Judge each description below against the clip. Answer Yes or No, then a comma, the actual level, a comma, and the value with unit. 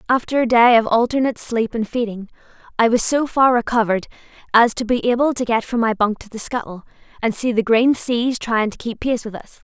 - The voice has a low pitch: No, high, 235 Hz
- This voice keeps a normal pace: No, fast, 225 wpm